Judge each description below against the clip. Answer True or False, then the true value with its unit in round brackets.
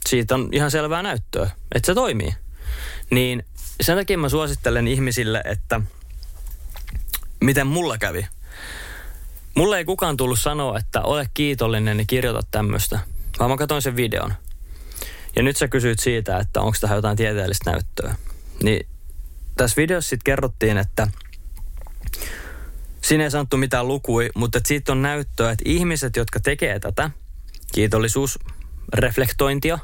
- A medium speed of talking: True (135 wpm)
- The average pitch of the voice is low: True (110 Hz)